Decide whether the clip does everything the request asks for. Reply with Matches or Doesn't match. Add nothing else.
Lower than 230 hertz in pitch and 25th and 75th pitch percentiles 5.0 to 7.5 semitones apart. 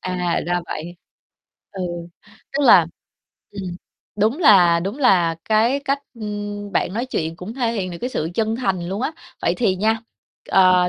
Doesn't match